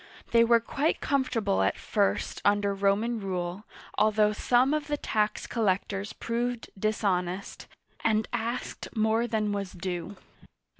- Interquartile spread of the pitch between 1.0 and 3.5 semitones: Yes, average, 2.9 semitones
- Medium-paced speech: No, slow, 130 wpm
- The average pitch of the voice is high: Yes, high, 215 Hz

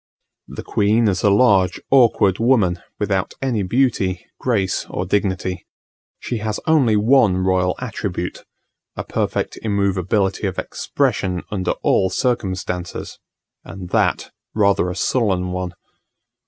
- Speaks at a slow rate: Yes, slow, 120 wpm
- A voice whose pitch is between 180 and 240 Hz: No, low, 100 Hz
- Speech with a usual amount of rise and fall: Yes, average, 3.4 semitones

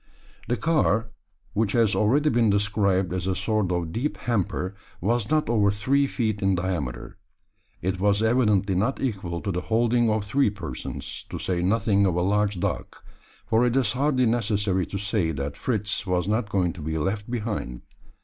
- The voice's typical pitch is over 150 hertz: No, low, 105 Hz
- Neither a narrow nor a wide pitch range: Yes, average, 3.7 semitones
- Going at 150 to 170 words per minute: No, average, 180 wpm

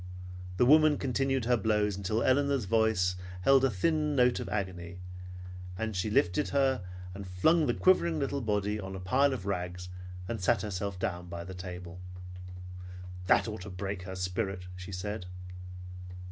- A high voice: No, low, 105 Hz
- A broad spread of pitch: Yes, wide, 6.1 semitones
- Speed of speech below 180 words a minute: Yes, average, 160 wpm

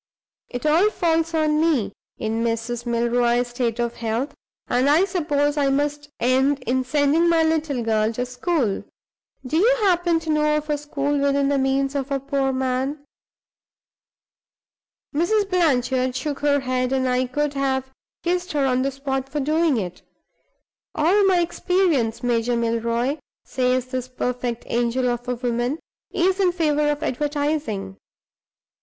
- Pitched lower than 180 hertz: No, very high, 275 Hz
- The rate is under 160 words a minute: Yes, average, 150 wpm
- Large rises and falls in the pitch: No, average, 3.6 semitones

